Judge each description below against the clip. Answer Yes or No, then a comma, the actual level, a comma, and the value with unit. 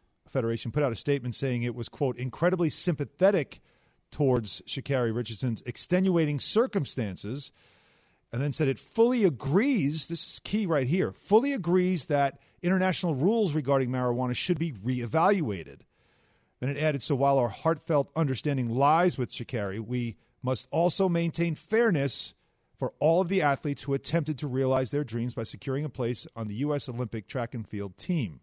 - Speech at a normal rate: Yes, average, 160 wpm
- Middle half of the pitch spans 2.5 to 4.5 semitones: No, wide, 5.5 semitones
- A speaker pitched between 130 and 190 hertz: Yes, medium, 140 Hz